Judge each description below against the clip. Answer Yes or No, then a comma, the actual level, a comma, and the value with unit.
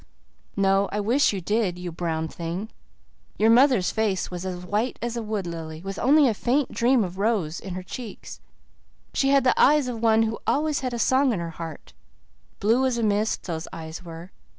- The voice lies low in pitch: No, high, 210 Hz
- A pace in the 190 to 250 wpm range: Yes, average, 200 wpm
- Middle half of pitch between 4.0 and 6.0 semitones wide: Yes, average, 5.2 semitones